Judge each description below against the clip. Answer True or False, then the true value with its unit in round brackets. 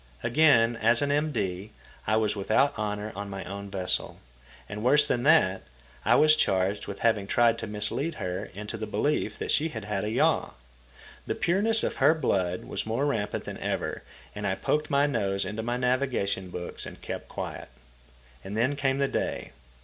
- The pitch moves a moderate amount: False (5.7 semitones)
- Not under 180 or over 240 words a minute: True (185 wpm)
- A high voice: False (110 Hz)